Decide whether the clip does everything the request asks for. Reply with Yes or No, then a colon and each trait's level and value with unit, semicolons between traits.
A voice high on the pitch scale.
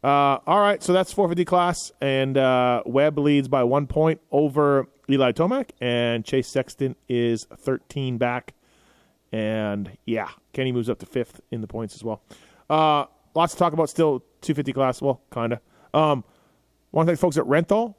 No: medium, 140 Hz